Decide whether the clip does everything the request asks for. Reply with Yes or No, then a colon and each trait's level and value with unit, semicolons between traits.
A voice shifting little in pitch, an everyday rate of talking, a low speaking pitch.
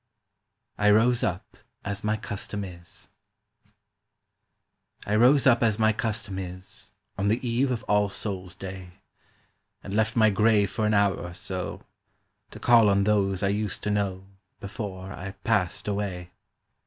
Yes: narrow, 2.3 semitones; average, 150 wpm; low, 100 Hz